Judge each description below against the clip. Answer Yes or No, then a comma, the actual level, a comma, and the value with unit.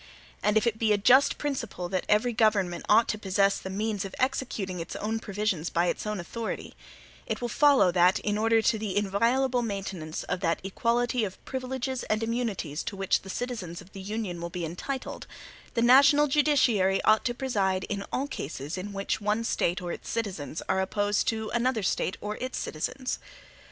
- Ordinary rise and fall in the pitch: Yes, average, 4.0 semitones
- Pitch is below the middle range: No, high, 210 Hz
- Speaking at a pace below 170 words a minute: No, average, 190 wpm